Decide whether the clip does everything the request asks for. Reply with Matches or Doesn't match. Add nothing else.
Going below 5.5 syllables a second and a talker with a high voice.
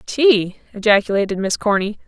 Matches